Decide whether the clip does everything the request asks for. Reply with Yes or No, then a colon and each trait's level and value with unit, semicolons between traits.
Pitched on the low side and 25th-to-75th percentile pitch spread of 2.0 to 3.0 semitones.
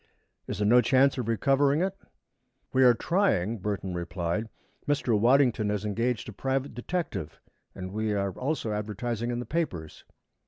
No: low, 115 Hz; average, 4.6 semitones